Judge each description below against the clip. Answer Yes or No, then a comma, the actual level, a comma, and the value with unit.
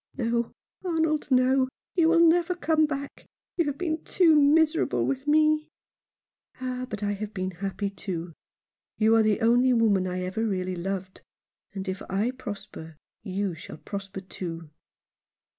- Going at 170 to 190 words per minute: No, average, 155 wpm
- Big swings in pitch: Yes, wide, 7.6 semitones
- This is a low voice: No, high, 225 Hz